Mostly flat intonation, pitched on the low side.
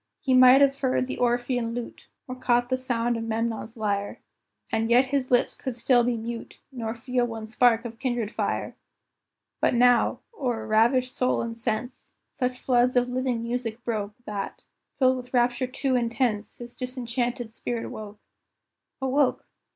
No: narrow, 1.8 semitones; high, 245 Hz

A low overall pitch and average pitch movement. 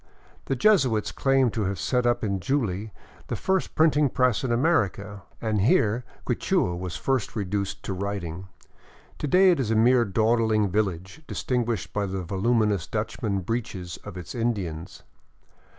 Yes: low, 110 Hz; average, 4.5 semitones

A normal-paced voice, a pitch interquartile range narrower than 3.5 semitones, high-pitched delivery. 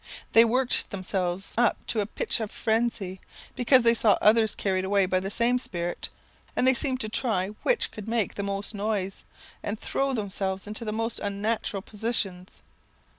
Yes: average, 175 wpm; average, 3.1 semitones; high, 215 Hz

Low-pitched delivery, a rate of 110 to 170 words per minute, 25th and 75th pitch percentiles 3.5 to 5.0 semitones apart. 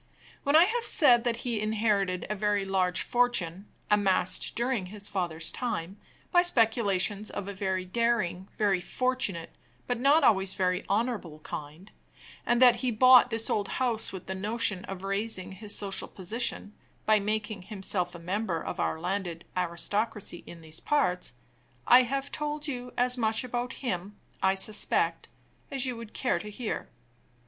No: high, 210 Hz; average, 160 wpm; average, 4.3 semitones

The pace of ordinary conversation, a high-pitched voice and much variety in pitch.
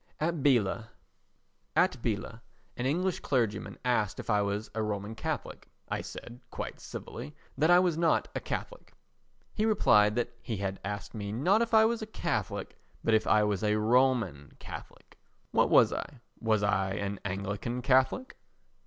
No: average, 160 wpm; low, 115 Hz; wide, 6.0 semitones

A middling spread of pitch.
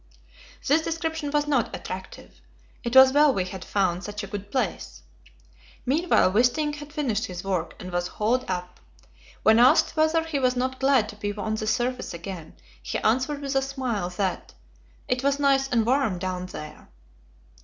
No: wide, 6.3 semitones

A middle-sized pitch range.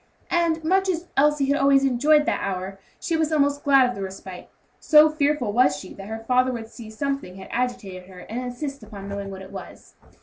No: wide, 6.9 semitones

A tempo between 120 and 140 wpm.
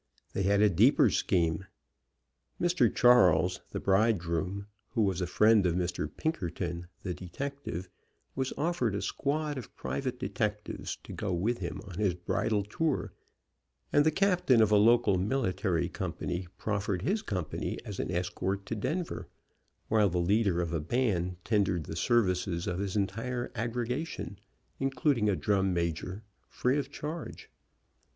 No: average, 150 wpm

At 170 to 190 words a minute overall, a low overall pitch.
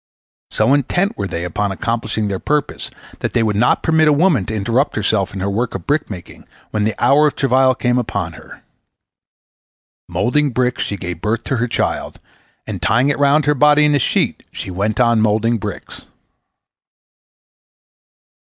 Yes: average, 175 wpm; low, 115 Hz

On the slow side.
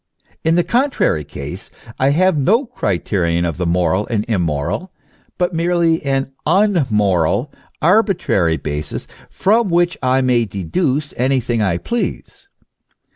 Yes: slow, 125 wpm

